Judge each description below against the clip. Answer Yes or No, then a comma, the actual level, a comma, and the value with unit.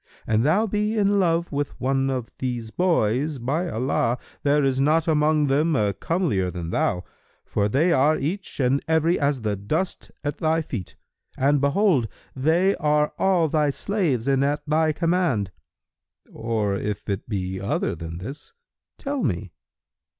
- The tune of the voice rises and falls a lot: Yes, wide, 6.1 semitones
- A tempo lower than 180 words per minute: Yes, average, 155 wpm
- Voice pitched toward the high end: No, medium, 145 Hz